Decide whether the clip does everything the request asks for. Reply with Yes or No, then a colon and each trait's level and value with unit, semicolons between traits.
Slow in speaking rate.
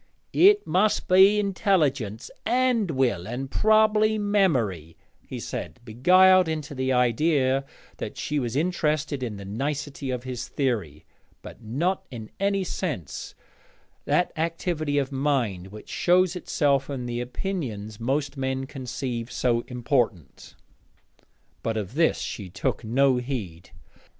Yes: slow, 130 wpm